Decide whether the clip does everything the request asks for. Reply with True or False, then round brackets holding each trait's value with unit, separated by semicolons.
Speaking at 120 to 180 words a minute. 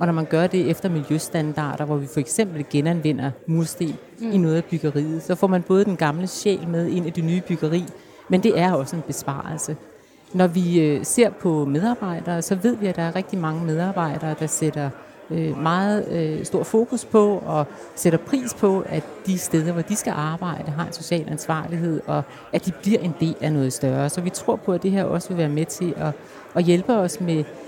False (210 wpm)